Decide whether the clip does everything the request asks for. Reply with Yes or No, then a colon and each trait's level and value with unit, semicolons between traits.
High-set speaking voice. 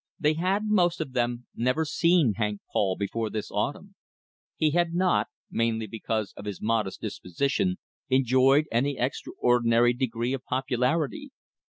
No: low, 125 Hz